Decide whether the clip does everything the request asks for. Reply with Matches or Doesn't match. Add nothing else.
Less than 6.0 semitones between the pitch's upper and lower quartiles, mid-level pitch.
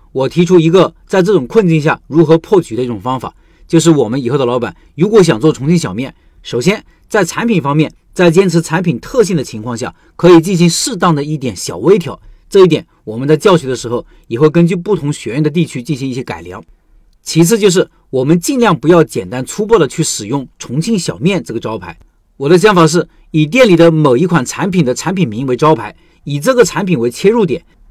Matches